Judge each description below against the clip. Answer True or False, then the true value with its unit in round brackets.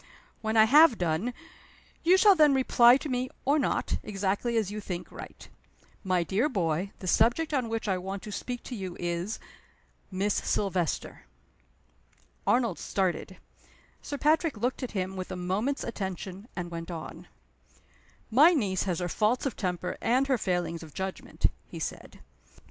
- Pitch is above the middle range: True (205 Hz)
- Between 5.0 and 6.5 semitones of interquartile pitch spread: True (5.4 semitones)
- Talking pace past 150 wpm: True (160 wpm)